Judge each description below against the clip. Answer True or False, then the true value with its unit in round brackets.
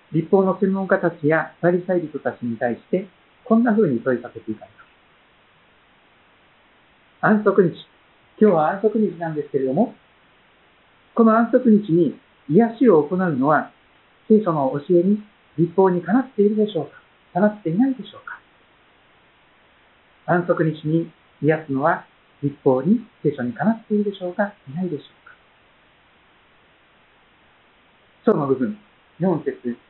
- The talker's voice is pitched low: False (180 Hz)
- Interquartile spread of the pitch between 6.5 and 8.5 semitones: False (5.8 semitones)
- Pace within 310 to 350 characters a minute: False (280 characters per minute)